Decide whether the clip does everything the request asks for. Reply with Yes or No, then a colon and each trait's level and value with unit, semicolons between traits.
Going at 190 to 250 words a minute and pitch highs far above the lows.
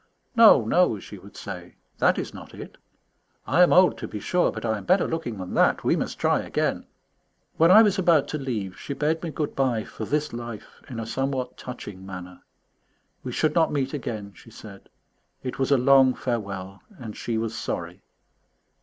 Yes: average, 195 wpm; wide, 6.3 semitones